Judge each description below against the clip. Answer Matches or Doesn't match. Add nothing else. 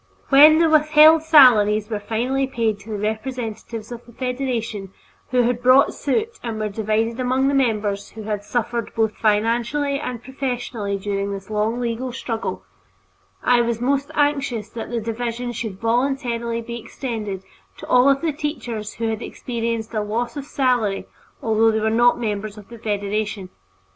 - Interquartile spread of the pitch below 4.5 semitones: Matches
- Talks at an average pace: Matches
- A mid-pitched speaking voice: Doesn't match